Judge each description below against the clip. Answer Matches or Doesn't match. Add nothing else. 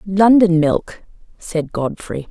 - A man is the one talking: Doesn't match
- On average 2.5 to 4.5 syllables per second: Matches